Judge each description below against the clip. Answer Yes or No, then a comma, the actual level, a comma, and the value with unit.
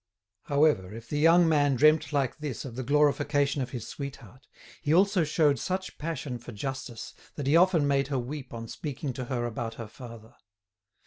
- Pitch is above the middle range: No, medium, 140 Hz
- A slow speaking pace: No, average, 185 wpm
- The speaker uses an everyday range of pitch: Yes, average, 3.8 semitones